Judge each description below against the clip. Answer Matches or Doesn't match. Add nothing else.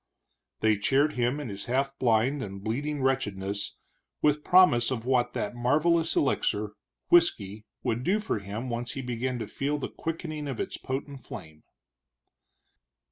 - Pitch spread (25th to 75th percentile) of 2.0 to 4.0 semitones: Doesn't match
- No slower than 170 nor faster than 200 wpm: Doesn't match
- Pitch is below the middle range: Matches